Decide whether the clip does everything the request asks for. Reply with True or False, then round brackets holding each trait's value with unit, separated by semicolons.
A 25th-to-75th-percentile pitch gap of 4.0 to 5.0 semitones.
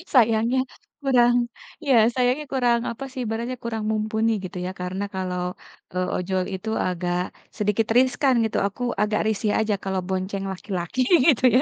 True (4.5 semitones)